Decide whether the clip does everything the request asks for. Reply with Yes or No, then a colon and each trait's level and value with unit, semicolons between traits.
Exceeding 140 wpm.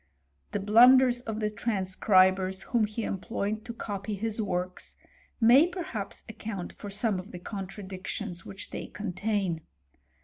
No: slow, 135 wpm